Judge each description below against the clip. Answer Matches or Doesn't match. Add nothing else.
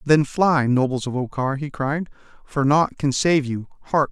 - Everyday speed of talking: Matches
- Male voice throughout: Matches